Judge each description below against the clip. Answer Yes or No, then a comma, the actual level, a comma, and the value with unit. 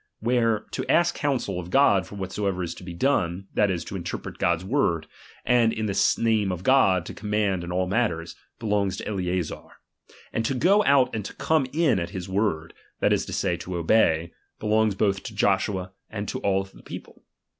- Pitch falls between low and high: No, low, 100 Hz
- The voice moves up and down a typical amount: Yes, average, 3.8 semitones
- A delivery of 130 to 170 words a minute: No, average, 200 wpm